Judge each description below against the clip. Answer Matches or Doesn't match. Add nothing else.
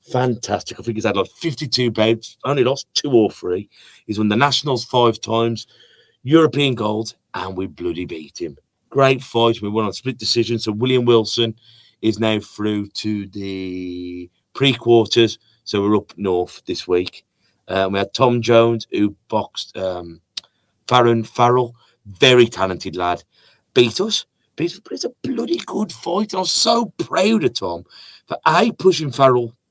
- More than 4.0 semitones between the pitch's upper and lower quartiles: Doesn't match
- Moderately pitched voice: Doesn't match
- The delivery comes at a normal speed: Matches